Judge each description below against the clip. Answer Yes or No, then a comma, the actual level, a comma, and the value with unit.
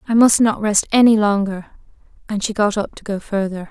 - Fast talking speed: Yes, fast, 210 wpm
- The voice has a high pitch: Yes, high, 210 Hz